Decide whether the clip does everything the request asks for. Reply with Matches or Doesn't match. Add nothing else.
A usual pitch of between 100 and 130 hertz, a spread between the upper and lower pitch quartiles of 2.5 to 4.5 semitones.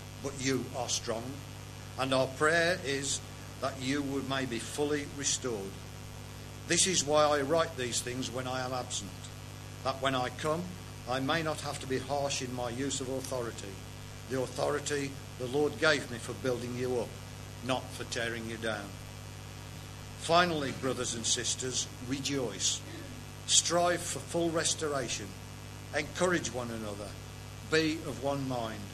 Matches